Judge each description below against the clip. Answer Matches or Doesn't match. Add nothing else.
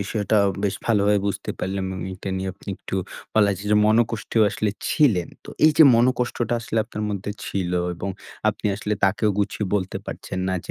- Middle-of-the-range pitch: Doesn't match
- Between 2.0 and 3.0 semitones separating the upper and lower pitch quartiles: Matches